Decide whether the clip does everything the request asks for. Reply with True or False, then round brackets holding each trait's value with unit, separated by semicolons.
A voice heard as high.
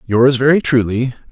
False (125 Hz)